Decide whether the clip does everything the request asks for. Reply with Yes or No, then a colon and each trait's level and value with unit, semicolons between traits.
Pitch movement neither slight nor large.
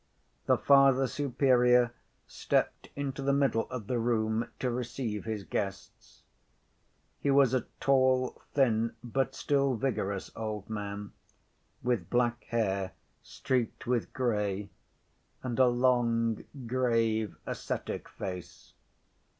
Yes: average, 3.0 semitones